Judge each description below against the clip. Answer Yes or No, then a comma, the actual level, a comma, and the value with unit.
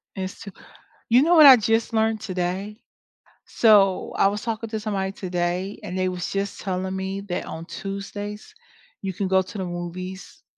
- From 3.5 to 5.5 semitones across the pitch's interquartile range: No, narrow, 2.5 semitones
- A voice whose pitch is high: Yes, high, 195 Hz